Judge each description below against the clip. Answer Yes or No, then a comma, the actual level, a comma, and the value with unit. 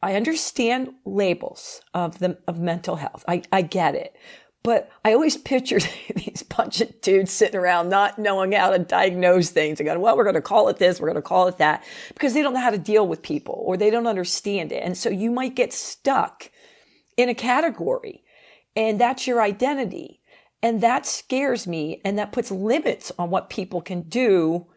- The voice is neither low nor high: No, high, 215 Hz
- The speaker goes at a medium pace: Yes, average, 195 wpm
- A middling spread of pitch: No, wide, 5.7 semitones